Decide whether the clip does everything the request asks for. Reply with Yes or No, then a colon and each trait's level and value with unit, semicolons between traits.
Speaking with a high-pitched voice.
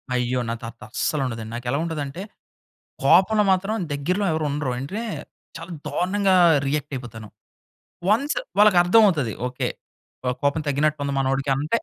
No: medium, 150 Hz